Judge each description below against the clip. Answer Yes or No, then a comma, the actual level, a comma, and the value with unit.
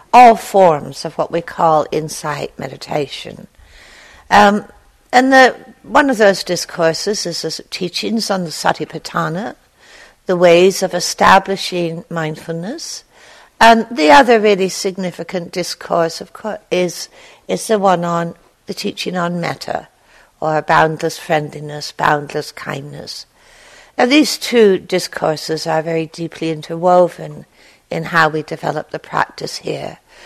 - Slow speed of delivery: Yes, slow, 125 wpm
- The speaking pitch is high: No, medium, 175 Hz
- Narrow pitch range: No, average, 4.0 semitones